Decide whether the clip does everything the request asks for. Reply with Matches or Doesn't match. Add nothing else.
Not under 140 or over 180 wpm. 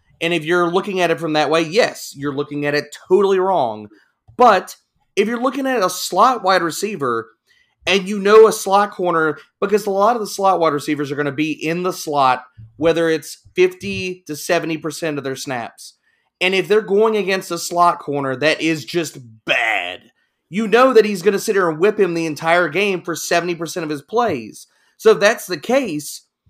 Doesn't match